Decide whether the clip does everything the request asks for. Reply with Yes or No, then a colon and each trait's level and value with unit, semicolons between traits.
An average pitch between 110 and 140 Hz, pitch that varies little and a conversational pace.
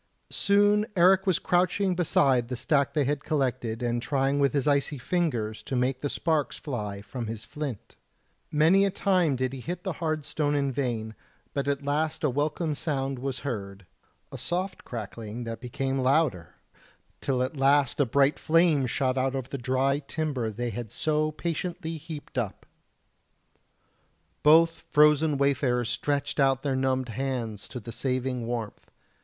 No: low, 135 Hz; average, 3.8 semitones; average, 160 wpm